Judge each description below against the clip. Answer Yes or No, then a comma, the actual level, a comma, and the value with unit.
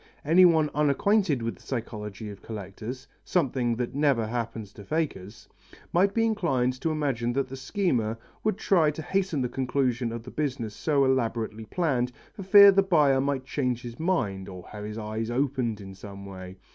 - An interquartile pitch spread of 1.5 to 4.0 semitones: No, wide, 5.5 semitones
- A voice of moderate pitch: No, low, 130 Hz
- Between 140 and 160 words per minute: No, average, 175 wpm